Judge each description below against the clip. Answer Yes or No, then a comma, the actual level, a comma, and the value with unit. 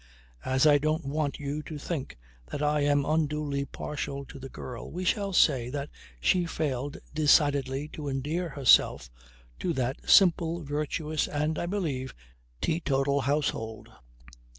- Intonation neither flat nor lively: No, narrow, 2.3 semitones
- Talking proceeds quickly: No, average, 140 wpm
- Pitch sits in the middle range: Yes, medium, 145 Hz